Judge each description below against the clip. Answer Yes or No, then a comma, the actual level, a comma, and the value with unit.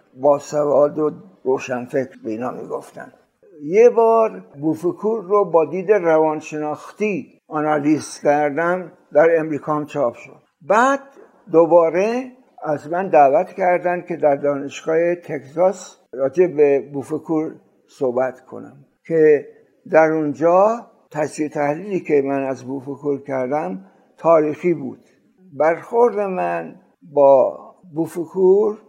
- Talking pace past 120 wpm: No, slow, 105 wpm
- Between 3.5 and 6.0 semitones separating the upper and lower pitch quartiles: Yes, average, 4.4 semitones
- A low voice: No, medium, 160 Hz